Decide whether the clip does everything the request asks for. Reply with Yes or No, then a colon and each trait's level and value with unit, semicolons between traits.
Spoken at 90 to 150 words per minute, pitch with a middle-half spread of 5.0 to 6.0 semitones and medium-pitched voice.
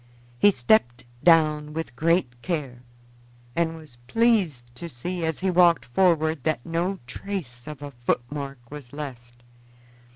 Yes: slow, 135 wpm; wide, 5.6 semitones; medium, 150 Hz